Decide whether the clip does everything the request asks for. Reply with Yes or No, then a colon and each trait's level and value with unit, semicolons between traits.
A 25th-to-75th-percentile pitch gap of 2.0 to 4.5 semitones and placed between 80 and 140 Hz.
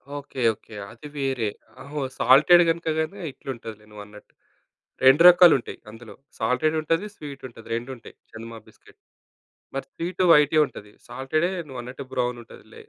No: average, 5.1 semitones; low, 135 Hz